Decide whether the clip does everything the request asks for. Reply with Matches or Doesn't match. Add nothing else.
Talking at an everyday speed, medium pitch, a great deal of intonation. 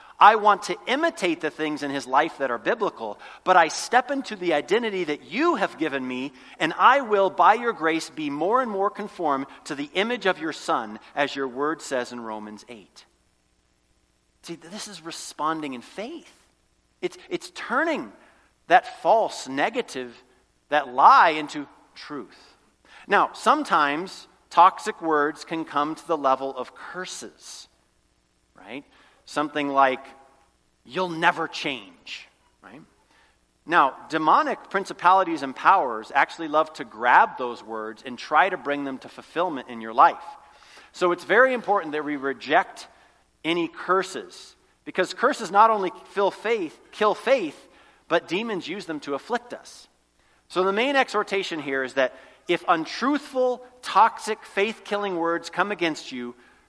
Matches